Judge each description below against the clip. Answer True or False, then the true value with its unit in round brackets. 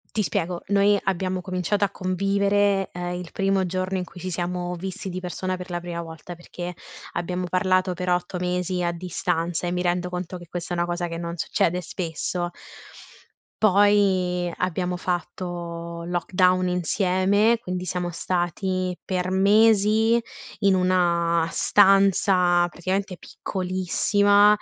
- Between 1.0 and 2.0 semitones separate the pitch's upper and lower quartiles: True (1.5 semitones)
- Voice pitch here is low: False (180 Hz)